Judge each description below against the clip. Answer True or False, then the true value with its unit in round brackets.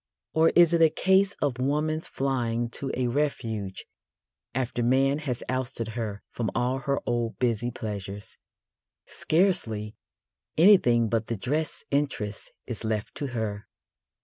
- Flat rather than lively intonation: False (4.4 semitones)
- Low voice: True (125 Hz)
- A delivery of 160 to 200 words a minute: False (135 wpm)